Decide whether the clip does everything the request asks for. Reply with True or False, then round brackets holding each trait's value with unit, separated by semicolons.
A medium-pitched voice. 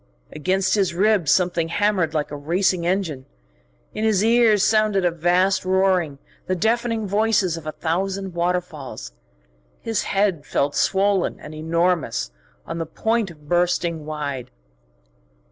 True (180 Hz)